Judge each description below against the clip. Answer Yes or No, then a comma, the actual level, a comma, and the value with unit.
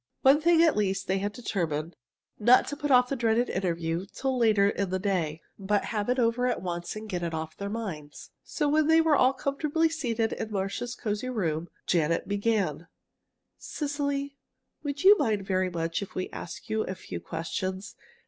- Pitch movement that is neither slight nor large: No, wide, 5.8 semitones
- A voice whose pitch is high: Yes, high, 210 Hz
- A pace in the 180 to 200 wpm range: Yes, average, 185 wpm